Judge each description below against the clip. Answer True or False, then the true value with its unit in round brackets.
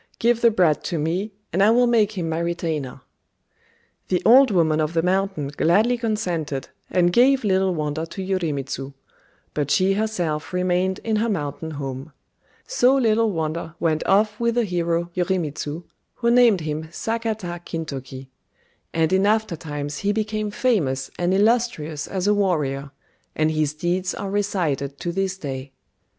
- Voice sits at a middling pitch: True (180 Hz)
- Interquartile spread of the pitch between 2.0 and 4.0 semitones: False (5.3 semitones)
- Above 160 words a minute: False (155 wpm)